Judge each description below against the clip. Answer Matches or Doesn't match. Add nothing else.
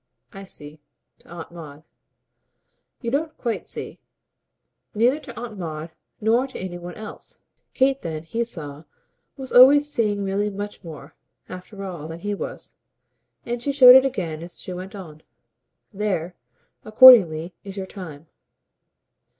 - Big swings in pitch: Matches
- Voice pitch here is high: Matches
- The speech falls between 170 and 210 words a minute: Doesn't match